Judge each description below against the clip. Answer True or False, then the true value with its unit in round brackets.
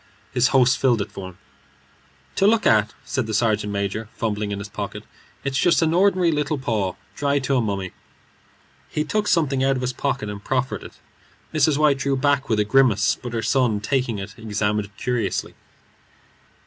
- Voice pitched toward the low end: True (125 Hz)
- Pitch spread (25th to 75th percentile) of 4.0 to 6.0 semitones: True (4.9 semitones)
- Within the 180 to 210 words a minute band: True (185 wpm)